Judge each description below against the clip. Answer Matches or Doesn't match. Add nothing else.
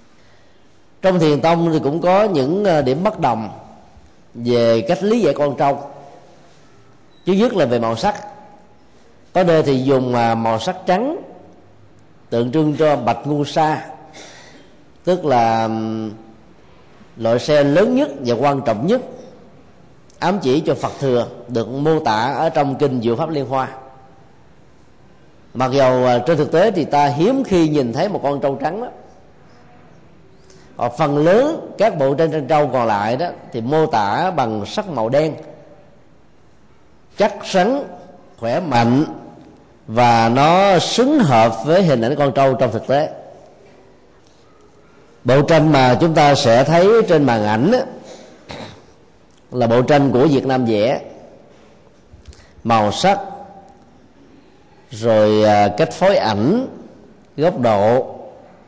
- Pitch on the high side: Doesn't match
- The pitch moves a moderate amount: Doesn't match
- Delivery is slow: Matches